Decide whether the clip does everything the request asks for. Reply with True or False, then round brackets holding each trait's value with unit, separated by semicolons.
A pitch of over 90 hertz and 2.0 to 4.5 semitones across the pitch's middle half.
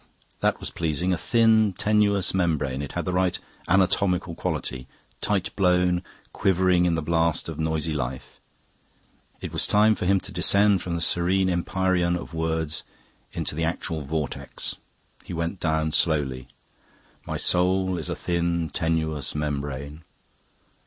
False (85 Hz; 2.9 semitones)